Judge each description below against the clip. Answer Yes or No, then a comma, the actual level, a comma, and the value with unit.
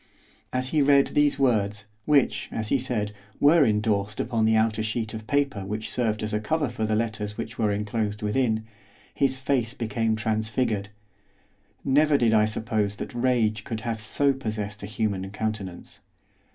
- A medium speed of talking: Yes, average, 165 wpm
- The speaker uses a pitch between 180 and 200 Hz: No, low, 110 Hz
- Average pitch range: Yes, average, 3.1 semitones